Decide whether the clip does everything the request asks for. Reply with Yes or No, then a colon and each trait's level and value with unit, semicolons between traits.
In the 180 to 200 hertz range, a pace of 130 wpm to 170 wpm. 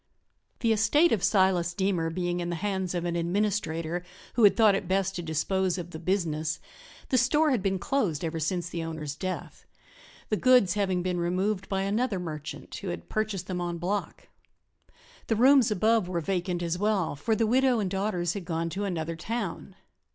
No: medium, 185 Hz; average, 185 wpm